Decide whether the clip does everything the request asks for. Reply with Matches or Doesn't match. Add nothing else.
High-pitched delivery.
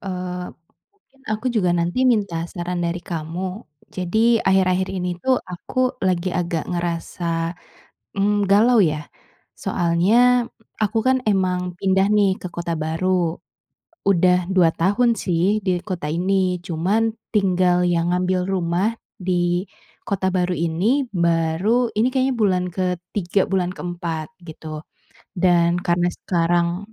Doesn't match